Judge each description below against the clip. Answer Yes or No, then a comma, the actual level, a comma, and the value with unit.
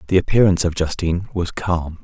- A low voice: Yes, very low, 85 Hz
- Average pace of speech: Yes, average, 175 wpm